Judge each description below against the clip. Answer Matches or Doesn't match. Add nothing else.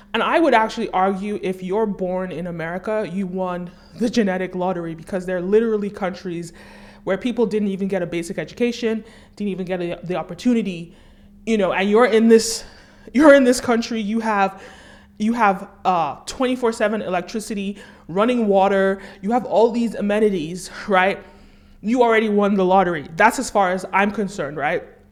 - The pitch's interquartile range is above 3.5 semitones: Doesn't match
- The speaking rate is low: Doesn't match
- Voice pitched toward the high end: Matches